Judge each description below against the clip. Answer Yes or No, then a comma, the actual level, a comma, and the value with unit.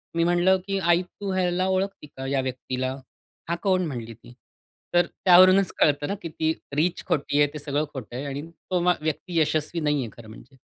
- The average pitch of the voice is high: No, medium, 160 Hz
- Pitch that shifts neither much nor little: Yes, average, 4.7 semitones